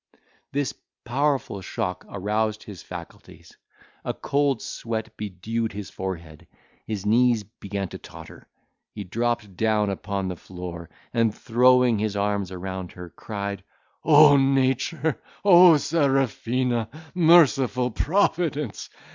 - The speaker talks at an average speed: No, slow, 110 wpm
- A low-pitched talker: Yes, low, 110 Hz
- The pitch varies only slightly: No, average, 5.2 semitones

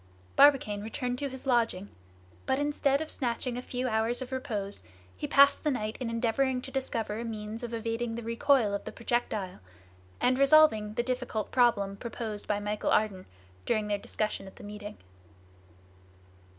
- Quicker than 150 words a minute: Yes, average, 165 wpm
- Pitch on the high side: Yes, high, 230 Hz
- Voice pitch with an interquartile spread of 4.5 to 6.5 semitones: No, average, 3.4 semitones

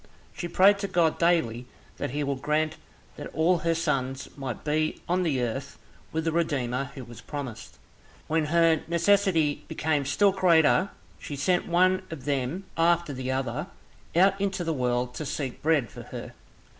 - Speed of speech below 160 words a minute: No, average, 170 wpm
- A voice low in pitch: No, medium, 155 Hz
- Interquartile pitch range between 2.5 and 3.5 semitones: No, average, 4.2 semitones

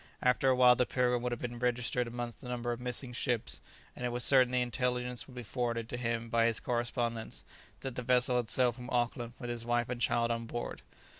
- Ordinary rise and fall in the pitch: No, narrow, 0.8 semitones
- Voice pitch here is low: Yes, low, 120 Hz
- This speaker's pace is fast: Yes, fast, 230 wpm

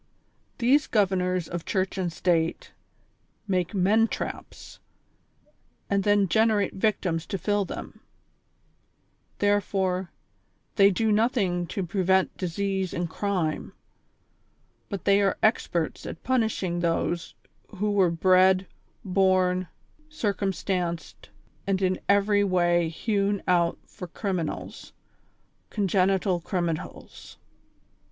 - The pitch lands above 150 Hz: Yes, high, 190 Hz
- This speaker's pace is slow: Yes, slow, 100 wpm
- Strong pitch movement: No, narrow, 2.4 semitones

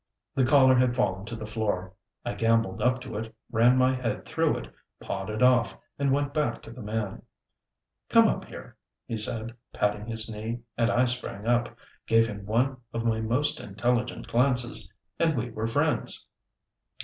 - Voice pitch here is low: Yes, low, 115 Hz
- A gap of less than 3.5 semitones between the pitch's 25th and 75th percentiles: Yes, narrow, 2.5 semitones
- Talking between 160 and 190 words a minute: Yes, average, 175 wpm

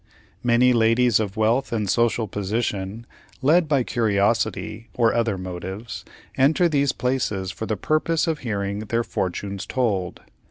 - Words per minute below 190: Yes, slow, 135 wpm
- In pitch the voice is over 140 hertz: No, low, 115 Hz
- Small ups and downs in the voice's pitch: No, average, 3.8 semitones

